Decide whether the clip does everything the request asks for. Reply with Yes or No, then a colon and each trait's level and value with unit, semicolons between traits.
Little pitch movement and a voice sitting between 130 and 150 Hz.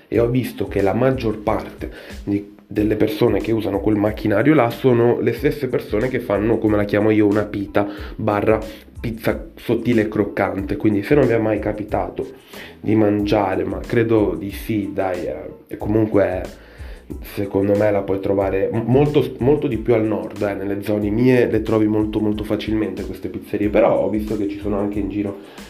No: narrow, 1.7 semitones; low, 105 Hz